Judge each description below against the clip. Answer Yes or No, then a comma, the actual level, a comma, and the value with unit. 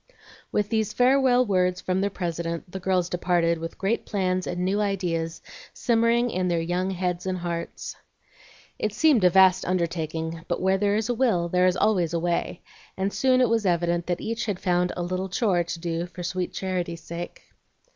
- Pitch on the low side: No, medium, 185 Hz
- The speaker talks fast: No, average, 190 wpm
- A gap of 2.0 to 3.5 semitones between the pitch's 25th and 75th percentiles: Yes, average, 2.8 semitones